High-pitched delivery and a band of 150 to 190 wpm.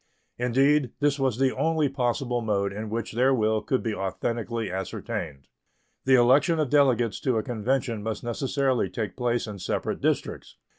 No: low, 120 Hz; average, 160 wpm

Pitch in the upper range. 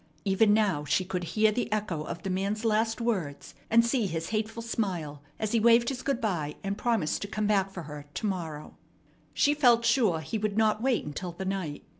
Yes: high, 210 Hz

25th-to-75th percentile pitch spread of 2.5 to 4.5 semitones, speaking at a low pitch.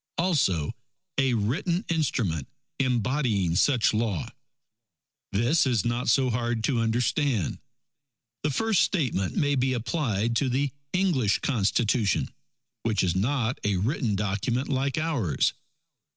No: average, 5.1 semitones; low, 120 Hz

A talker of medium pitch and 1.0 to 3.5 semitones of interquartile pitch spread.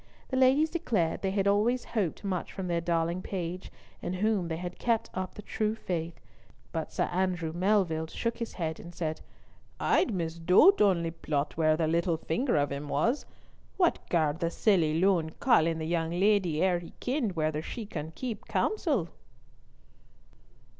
No: medium, 175 Hz; average, 4.5 semitones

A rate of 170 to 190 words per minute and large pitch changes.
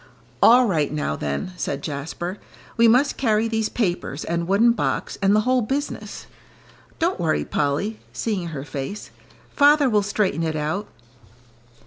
No: average, 145 wpm; wide, 6.6 semitones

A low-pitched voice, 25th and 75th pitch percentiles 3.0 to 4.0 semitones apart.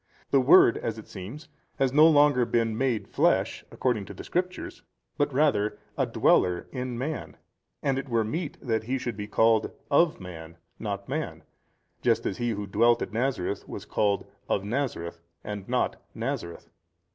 No: low, 115 Hz; average, 4.8 semitones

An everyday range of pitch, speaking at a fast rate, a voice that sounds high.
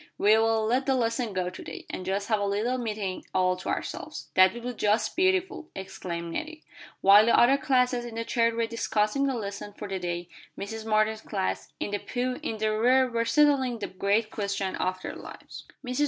Yes: average, 3.8 semitones; fast, 210 wpm; high, 220 Hz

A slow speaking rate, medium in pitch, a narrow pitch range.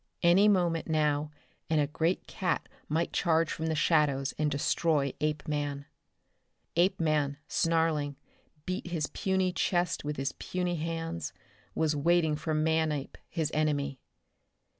Yes: slow, 125 wpm; medium, 155 Hz; narrow, 2.3 semitones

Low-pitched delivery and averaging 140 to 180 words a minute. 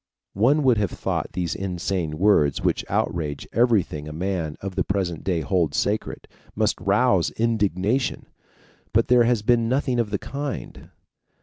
Yes: low, 100 Hz; average, 150 wpm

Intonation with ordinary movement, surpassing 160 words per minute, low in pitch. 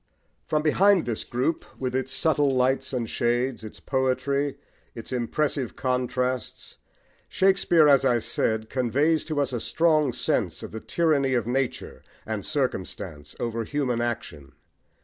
No: average, 3.5 semitones; average, 140 wpm; low, 130 Hz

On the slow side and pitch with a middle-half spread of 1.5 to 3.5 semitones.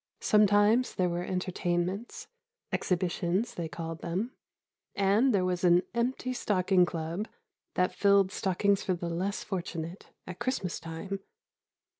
Yes: slow, 125 wpm; average, 2.7 semitones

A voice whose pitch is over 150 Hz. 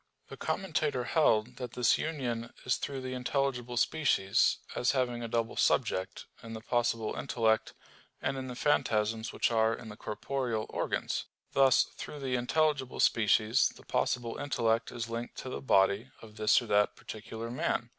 No: low, 120 Hz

